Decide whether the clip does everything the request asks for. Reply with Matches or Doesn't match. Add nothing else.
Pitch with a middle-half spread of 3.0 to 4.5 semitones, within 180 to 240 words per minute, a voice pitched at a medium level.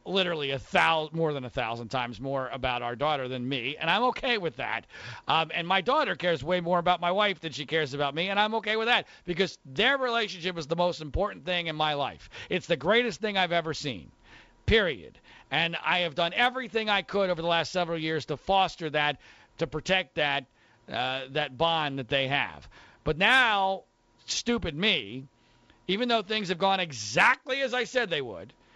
Doesn't match